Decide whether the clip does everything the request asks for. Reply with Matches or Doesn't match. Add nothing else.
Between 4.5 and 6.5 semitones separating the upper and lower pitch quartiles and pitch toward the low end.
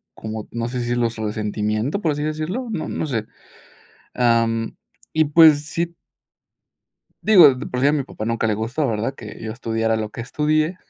Matches